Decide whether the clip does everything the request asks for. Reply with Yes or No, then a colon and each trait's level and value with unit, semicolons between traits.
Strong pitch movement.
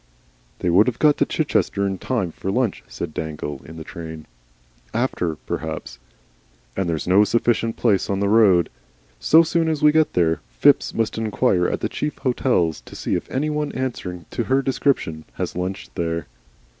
Yes: wide, 7.2 semitones